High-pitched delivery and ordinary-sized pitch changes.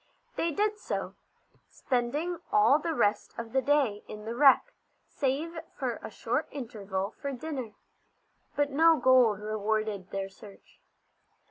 No: very high, 255 Hz; wide, 5.8 semitones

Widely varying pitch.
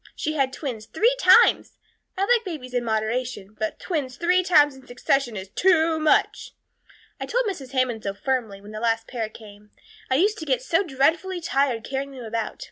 Yes: wide, 6.1 semitones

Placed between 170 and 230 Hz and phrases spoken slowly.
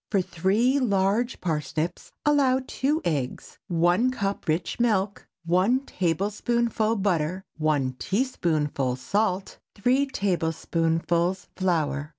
Yes: high, 190 Hz; slow, 100 wpm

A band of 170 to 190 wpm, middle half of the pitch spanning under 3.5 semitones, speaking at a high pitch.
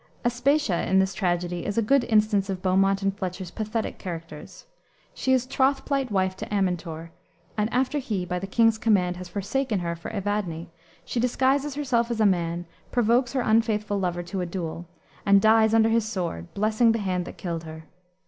No: average, 185 wpm; average, 4.4 semitones; high, 200 Hz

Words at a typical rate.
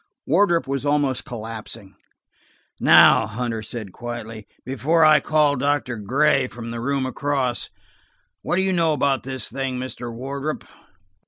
Yes: average, 145 wpm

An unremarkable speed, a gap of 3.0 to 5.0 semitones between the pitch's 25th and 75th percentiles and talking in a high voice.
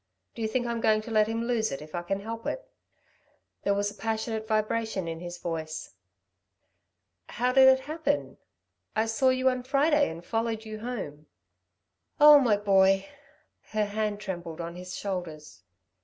Yes: average, 170 wpm; average, 4.1 semitones; high, 215 Hz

